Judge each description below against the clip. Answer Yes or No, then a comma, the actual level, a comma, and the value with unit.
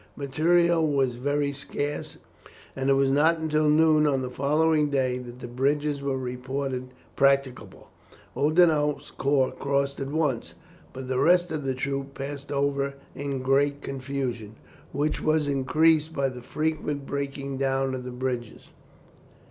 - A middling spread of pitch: No, narrow, 2.0 semitones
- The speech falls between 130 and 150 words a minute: Yes, average, 145 wpm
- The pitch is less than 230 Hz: Yes, medium, 140 Hz